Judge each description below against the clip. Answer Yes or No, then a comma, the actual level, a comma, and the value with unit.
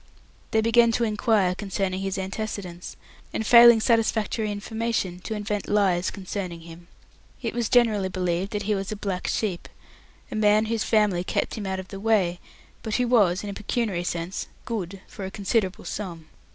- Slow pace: No, average, 175 wpm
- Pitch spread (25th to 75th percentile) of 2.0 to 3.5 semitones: Yes, average, 2.9 semitones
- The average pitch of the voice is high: Yes, high, 205 Hz